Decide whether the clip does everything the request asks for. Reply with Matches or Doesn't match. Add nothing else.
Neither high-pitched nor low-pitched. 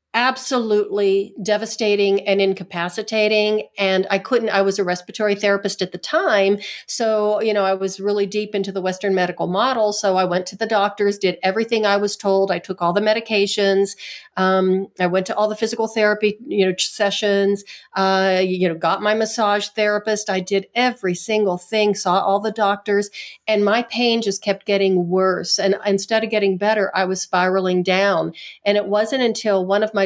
Doesn't match